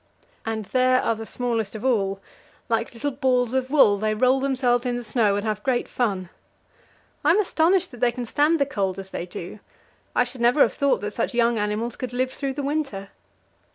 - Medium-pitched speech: No, high, 245 Hz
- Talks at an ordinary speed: No, fast, 210 wpm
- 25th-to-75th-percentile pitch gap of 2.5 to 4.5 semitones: Yes, average, 3.5 semitones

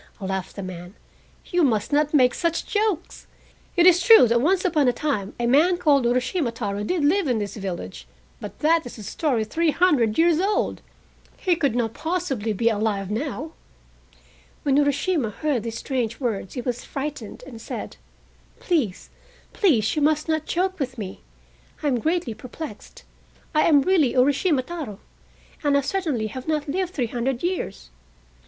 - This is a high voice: Yes, very high, 275 Hz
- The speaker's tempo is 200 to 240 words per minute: No, average, 170 wpm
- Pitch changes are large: Yes, wide, 6.5 semitones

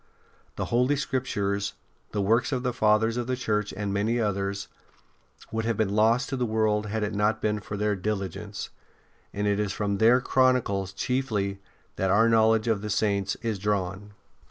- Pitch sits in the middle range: No, low, 105 Hz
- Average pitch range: No, narrow, 2.3 semitones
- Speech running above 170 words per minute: Yes, average, 180 wpm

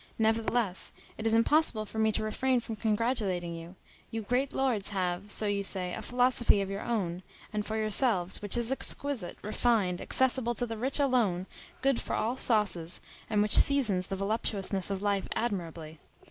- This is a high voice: Yes, high, 215 Hz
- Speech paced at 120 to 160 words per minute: No, average, 175 wpm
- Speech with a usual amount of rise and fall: Yes, average, 3.7 semitones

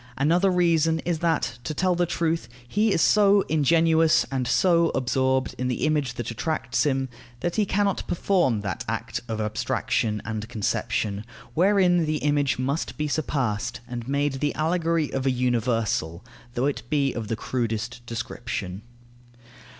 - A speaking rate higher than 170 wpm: No, average, 155 wpm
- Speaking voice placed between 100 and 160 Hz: Yes, medium, 140 Hz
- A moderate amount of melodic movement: No, wide, 5.8 semitones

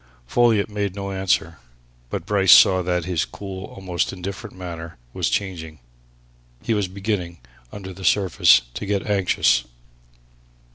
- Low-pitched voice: Yes, very low, 95 Hz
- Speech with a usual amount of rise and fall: No, narrow, 2.3 semitones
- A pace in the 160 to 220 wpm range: No, slow, 135 wpm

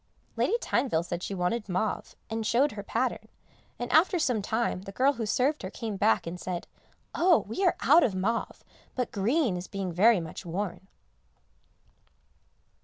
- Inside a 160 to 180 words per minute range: Yes, average, 170 wpm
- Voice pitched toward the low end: No, high, 215 Hz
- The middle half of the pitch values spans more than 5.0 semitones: Yes, wide, 5.4 semitones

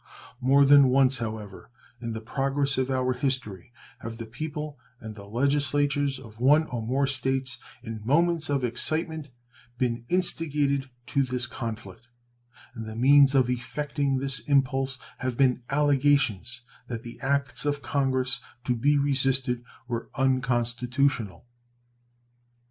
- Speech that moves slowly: Yes, slow, 130 wpm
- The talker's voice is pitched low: Yes, low, 130 Hz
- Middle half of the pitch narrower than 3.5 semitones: Yes, average, 2.8 semitones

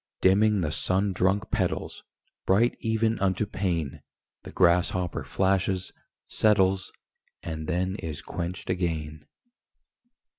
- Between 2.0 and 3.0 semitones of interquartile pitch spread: Yes, narrow, 2.5 semitones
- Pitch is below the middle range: Yes, very low, 95 Hz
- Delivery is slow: Yes, slow, 105 wpm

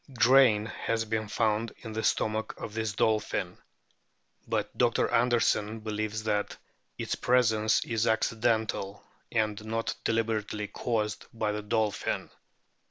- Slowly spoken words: Yes, slow, 120 wpm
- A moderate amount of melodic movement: No, narrow, 1.2 semitones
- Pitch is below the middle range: Yes, low, 110 Hz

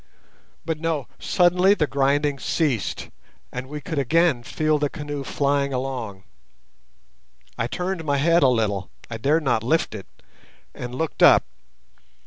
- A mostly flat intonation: No, average, 4.2 semitones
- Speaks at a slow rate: Yes, slow, 130 wpm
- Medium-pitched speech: Yes, medium, 145 Hz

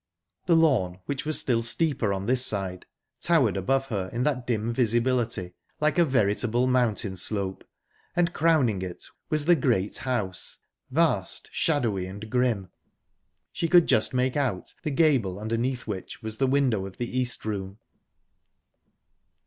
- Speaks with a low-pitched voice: Yes, low, 120 Hz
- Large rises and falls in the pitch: No, average, 5.0 semitones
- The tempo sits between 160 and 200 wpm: No, average, 150 wpm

